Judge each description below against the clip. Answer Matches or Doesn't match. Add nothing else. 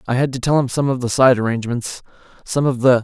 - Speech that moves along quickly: Matches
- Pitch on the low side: Matches